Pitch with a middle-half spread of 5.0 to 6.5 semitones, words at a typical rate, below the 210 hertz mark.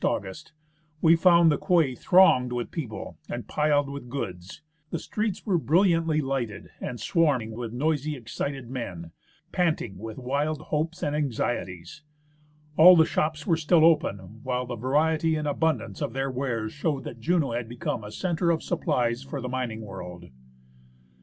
Yes: average, 5.3 semitones; average, 160 wpm; medium, 140 Hz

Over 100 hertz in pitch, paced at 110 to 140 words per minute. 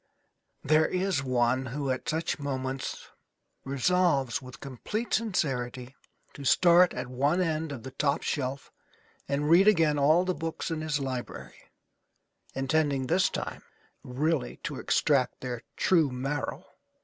Yes: medium, 140 Hz; slow, 135 wpm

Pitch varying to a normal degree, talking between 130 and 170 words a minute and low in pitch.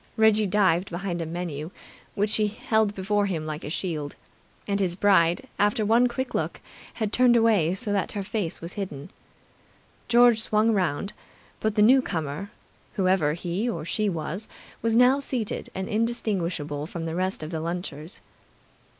No: average, 4.4 semitones; average, 160 wpm; high, 195 Hz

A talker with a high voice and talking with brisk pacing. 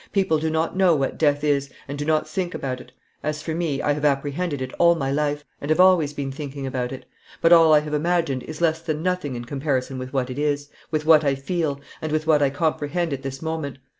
No: medium, 150 Hz; fast, 245 wpm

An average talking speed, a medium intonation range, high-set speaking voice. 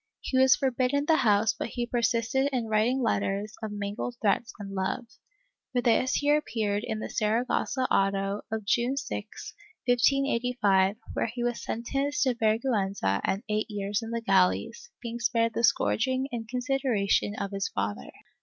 Yes: average, 160 wpm; average, 3.7 semitones; high, 230 Hz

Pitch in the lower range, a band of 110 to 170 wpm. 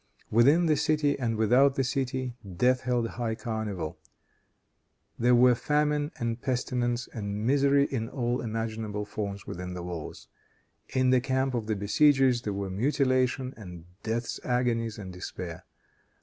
Yes: low, 120 Hz; average, 145 wpm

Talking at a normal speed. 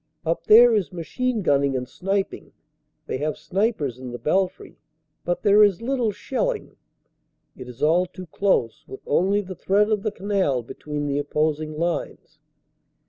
Yes: average, 160 wpm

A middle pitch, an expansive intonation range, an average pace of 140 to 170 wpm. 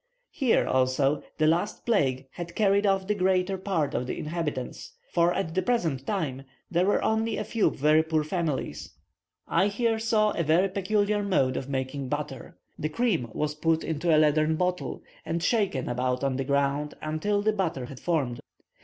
No: medium, 165 Hz; wide, 5.9 semitones; average, 180 wpm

